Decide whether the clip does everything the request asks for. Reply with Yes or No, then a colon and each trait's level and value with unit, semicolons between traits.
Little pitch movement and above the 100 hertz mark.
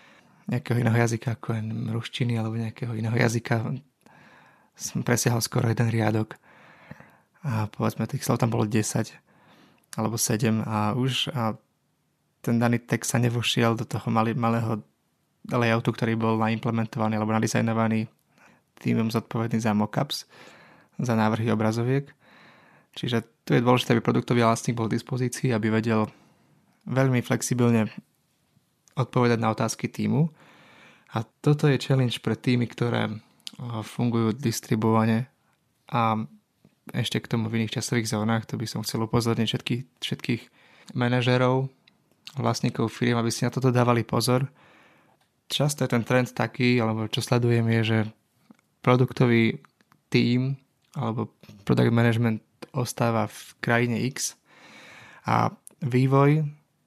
Yes: narrow, 2.0 semitones; low, 115 Hz